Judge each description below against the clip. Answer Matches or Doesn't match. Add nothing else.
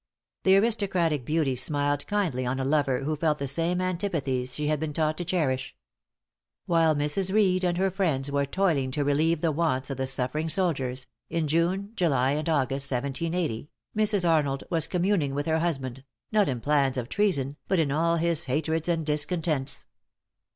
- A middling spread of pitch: Matches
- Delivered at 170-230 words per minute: Matches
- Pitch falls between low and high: Matches